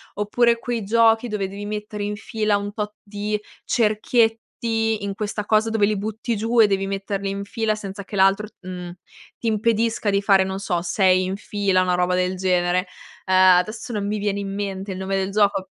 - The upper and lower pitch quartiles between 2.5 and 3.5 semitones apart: No, narrow, 1.9 semitones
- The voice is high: Yes, high, 205 Hz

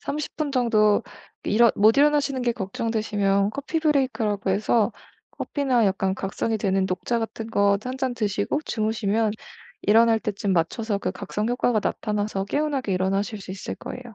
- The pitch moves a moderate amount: Yes, average, 3.6 semitones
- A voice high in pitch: Yes, high, 220 Hz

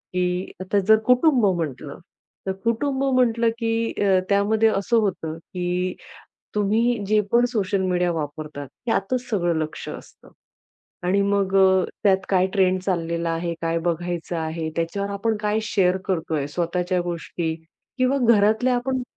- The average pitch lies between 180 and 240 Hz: Yes, high, 190 Hz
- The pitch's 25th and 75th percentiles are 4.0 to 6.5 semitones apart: Yes, average, 4.3 semitones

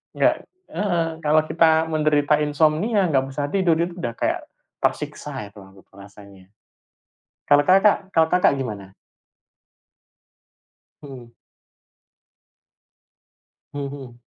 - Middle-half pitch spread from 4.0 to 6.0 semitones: Yes, average, 5.2 semitones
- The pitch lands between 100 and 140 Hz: No, medium, 150 Hz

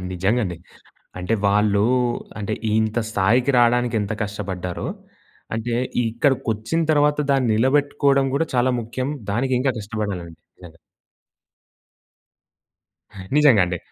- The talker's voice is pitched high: No, low, 115 Hz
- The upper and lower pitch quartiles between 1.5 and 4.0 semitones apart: No, average, 4.5 semitones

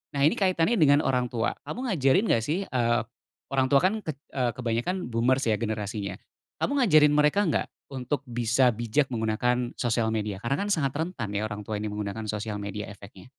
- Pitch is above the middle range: No, low, 125 Hz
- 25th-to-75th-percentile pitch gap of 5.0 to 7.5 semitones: Yes, average, 5.3 semitones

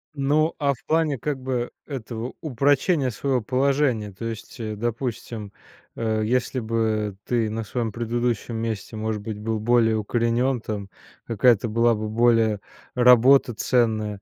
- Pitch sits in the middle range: No, low, 115 Hz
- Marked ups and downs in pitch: No, narrow, 2.6 semitones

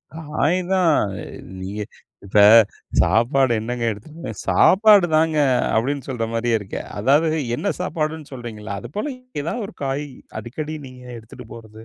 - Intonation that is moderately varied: No, wide, 5.7 semitones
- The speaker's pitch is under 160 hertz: Yes, low, 135 Hz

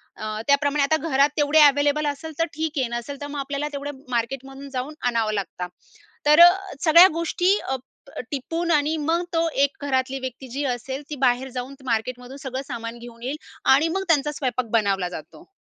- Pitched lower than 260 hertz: No, very high, 275 Hz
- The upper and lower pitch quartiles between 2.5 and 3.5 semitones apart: Yes, average, 3.2 semitones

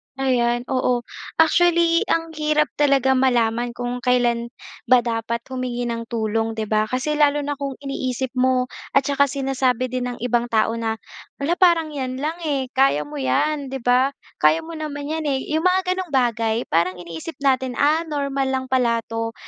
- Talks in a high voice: Yes, very high, 260 Hz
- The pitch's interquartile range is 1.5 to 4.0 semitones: Yes, average, 3.4 semitones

